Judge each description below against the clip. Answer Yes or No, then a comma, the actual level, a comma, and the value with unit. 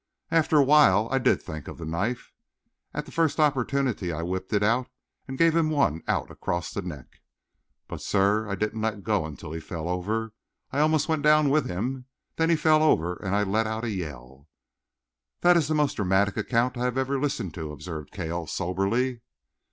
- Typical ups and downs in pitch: No, wide, 7.6 semitones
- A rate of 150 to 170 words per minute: No, average, 200 wpm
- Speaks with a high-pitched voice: No, low, 110 Hz